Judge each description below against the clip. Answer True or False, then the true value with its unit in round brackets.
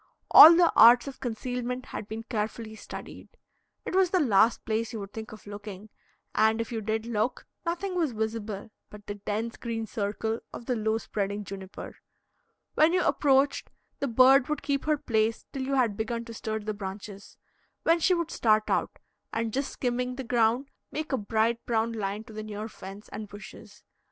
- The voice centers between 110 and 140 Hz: False (225 Hz)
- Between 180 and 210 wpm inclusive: True (185 wpm)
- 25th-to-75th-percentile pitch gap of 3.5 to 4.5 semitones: False (3.1 semitones)